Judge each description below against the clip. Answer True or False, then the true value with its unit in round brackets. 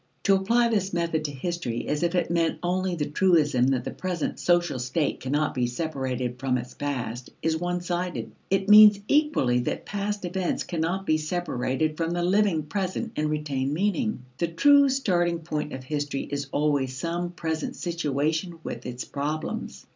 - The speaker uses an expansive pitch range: False (4.3 semitones)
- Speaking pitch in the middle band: True (165 Hz)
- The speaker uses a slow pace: False (170 wpm)